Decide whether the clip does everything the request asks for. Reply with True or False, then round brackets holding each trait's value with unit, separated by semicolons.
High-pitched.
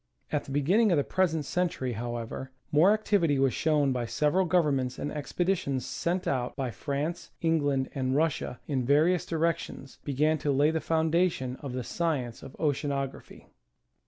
False (145 Hz)